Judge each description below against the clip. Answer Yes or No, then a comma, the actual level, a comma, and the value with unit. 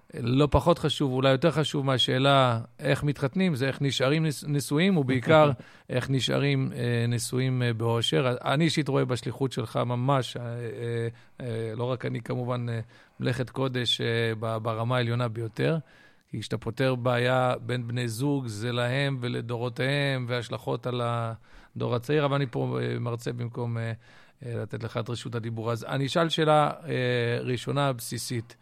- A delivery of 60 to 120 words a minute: No, average, 130 wpm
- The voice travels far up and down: No, average, 2.8 semitones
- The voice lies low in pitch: Yes, low, 125 Hz